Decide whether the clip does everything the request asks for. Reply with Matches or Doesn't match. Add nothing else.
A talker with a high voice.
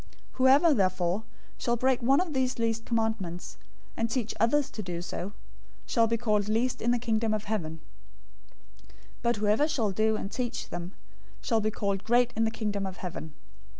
Matches